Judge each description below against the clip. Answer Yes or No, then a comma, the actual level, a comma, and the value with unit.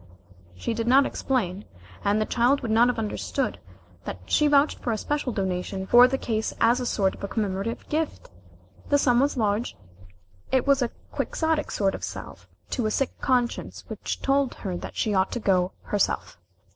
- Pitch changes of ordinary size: Yes, average, 4.8 semitones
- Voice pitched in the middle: No, high, 235 Hz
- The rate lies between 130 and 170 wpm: No, average, 185 wpm